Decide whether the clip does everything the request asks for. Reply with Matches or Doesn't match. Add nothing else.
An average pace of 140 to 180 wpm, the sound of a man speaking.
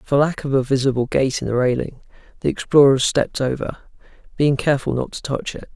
Doesn't match